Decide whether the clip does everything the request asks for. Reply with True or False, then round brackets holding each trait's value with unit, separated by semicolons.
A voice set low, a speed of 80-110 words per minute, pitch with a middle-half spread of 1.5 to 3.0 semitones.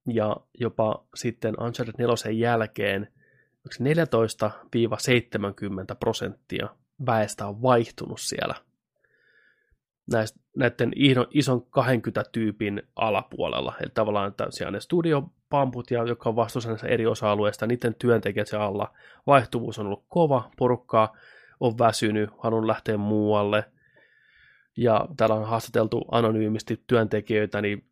True (115 Hz; 105 wpm; 2.4 semitones)